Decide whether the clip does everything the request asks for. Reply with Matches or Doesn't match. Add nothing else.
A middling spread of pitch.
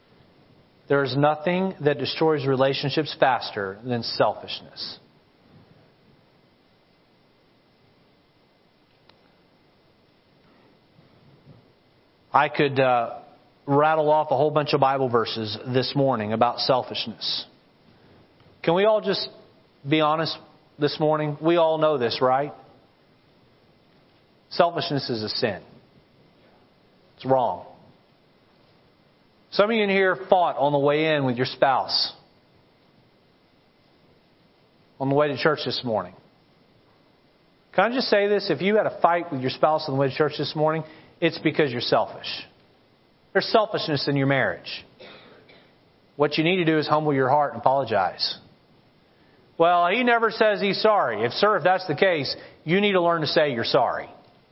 Matches